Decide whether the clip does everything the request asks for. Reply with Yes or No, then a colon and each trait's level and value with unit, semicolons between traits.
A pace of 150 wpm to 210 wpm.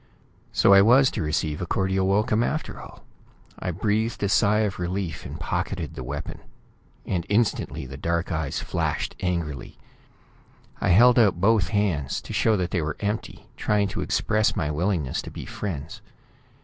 Yes: average, 165 wpm